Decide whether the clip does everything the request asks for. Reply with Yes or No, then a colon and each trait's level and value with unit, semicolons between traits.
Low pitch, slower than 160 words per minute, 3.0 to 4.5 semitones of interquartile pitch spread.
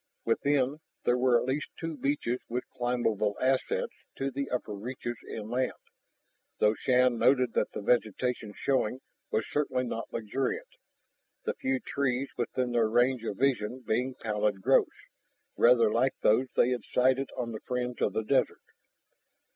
No: low, 125 Hz; average, 150 wpm; narrow, 2.5 semitones